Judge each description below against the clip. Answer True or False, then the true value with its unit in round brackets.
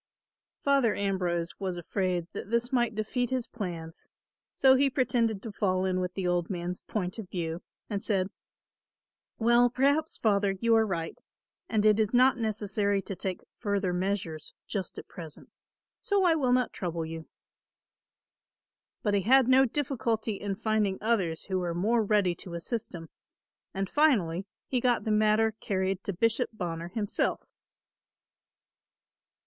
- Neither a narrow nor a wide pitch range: True (4.3 semitones)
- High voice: True (205 Hz)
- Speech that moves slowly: False (155 wpm)